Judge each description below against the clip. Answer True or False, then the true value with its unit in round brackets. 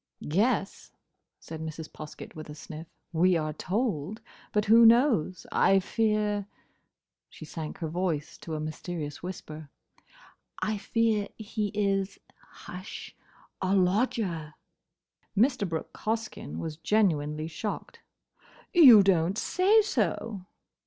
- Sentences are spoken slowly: True (105 wpm)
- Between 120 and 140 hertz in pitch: False (190 Hz)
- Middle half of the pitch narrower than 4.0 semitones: False (5.4 semitones)